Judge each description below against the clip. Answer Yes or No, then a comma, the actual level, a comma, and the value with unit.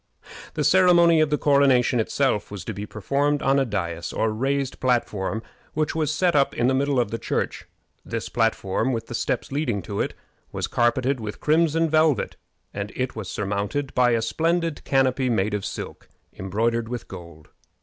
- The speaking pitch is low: Yes, low, 125 Hz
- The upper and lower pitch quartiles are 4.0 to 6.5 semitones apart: Yes, average, 5.2 semitones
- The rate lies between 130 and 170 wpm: No, average, 180 wpm